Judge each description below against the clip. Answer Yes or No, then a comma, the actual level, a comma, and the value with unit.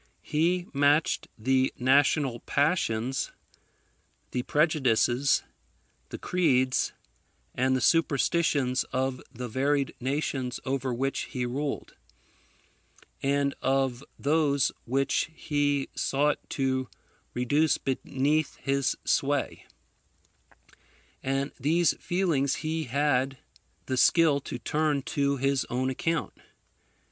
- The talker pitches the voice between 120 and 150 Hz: Yes, low, 135 Hz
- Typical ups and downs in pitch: No, narrow, 2.3 semitones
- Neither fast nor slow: No, slow, 95 wpm